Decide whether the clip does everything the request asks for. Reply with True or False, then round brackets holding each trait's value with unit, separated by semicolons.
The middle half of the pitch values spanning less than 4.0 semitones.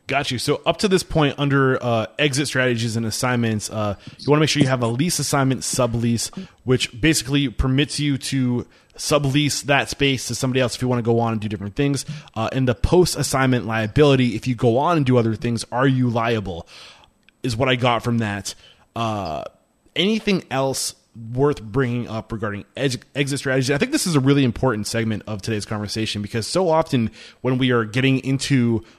True (3.5 semitones)